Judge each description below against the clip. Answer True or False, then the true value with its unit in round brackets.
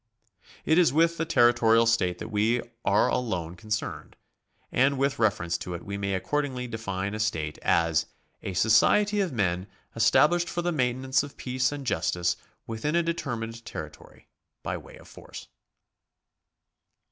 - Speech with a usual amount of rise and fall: False (6.1 semitones)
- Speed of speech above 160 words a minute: False (155 wpm)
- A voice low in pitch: True (115 Hz)